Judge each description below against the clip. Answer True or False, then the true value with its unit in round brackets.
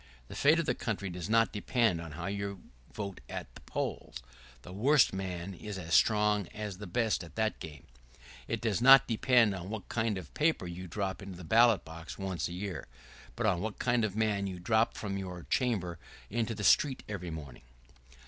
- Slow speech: False (205 wpm)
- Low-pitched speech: True (100 Hz)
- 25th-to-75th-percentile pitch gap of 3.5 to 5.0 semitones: True (3.8 semitones)